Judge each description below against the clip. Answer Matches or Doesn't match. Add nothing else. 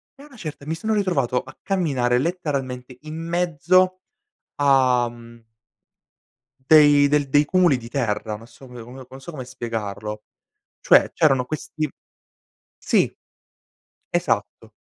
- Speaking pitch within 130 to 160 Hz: Matches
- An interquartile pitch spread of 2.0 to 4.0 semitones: Doesn't match